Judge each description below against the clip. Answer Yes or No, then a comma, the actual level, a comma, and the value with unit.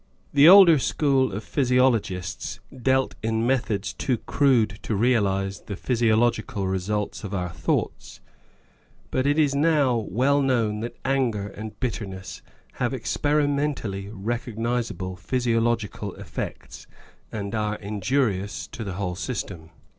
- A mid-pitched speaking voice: No, low, 115 Hz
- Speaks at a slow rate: Yes, slow, 125 wpm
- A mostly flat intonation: No, average, 4.6 semitones